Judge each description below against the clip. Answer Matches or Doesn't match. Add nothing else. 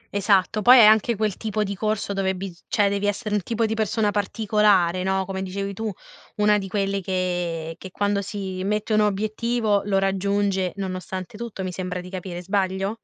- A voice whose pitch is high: Matches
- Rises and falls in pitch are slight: Matches